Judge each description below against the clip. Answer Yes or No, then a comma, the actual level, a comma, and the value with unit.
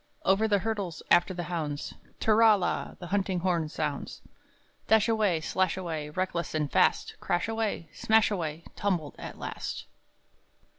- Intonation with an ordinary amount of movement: Yes, average, 4.1 semitones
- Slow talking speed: Yes, slow, 120 wpm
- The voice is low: No, medium, 185 Hz